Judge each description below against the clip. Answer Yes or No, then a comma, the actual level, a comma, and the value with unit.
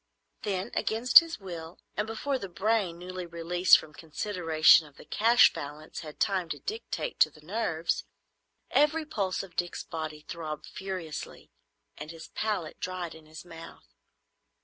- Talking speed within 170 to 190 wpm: No, average, 150 wpm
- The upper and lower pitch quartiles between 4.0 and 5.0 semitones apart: Yes, average, 4.6 semitones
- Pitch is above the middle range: No, medium, 175 Hz